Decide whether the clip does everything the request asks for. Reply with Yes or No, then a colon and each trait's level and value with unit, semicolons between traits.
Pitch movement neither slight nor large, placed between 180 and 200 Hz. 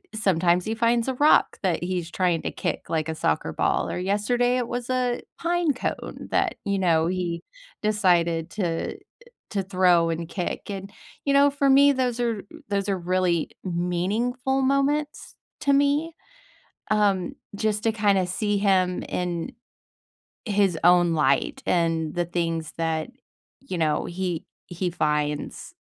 No: wide, 5.8 semitones; high, 190 Hz